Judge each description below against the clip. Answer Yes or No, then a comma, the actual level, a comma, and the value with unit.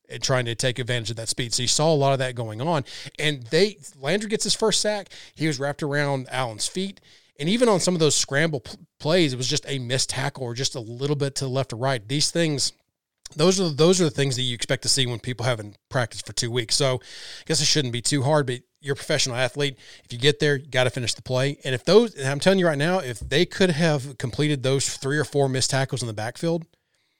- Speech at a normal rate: No, fast, 265 wpm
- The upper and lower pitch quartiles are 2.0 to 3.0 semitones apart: No, average, 3.7 semitones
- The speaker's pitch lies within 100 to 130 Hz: No, medium, 140 Hz